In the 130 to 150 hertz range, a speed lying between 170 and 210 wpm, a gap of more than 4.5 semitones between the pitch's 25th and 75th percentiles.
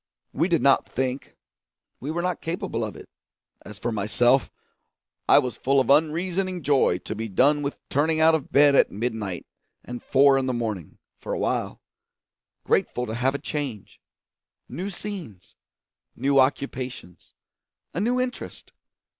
No: low, 135 Hz; average, 155 wpm; average, 5.2 semitones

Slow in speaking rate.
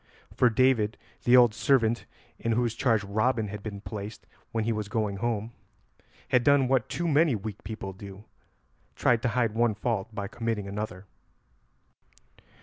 No: average, 155 wpm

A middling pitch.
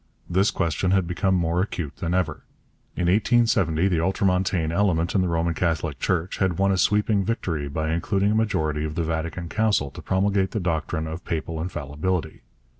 No: very low, 90 Hz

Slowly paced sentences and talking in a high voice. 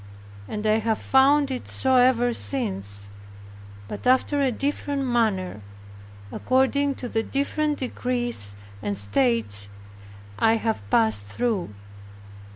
Yes: slow, 115 wpm; high, 235 Hz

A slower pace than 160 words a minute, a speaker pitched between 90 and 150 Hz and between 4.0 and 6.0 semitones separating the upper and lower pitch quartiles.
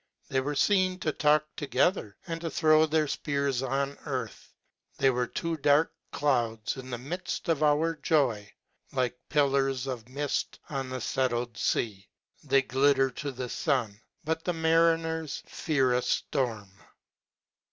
No: average, 150 wpm; medium, 140 Hz; average, 3.6 semitones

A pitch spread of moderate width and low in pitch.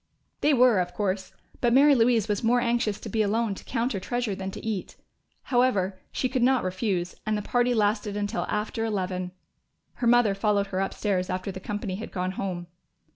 No: average, 4.0 semitones; high, 210 Hz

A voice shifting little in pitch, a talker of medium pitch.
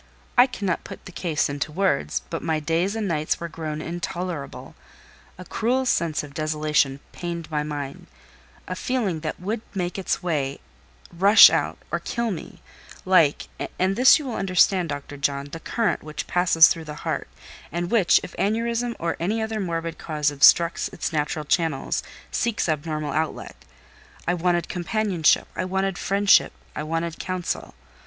No: average, 4.1 semitones; medium, 170 Hz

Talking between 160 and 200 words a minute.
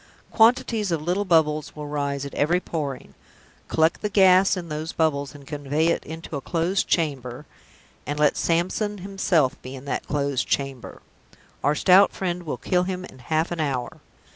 Yes: average, 170 wpm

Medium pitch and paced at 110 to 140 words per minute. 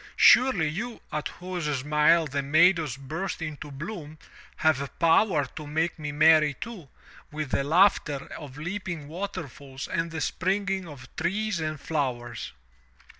Yes: medium, 155 Hz; slow, 135 wpm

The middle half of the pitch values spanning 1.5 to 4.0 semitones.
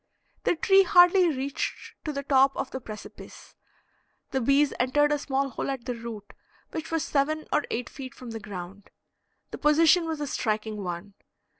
No: average, 4.7 semitones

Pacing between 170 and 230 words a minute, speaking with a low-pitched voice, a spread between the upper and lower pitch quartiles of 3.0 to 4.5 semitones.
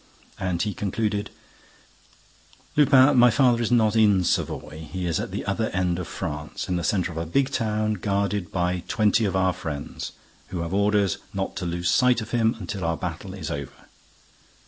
Yes: average, 185 wpm; very low, 95 Hz; average, 4.0 semitones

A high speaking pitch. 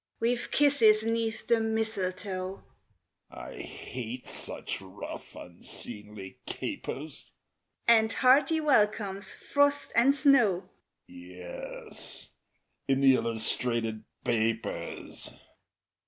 Yes: high, 195 Hz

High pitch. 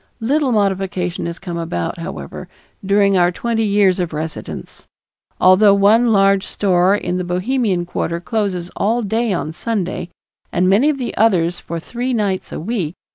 Yes: high, 195 Hz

